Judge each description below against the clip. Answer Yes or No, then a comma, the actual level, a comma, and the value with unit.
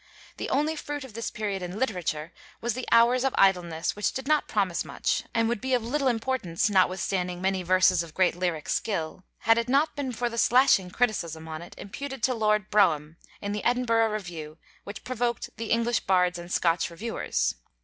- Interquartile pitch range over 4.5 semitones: Yes, average, 5.2 semitones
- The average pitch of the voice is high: Yes, high, 210 Hz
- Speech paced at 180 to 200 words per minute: Yes, average, 190 wpm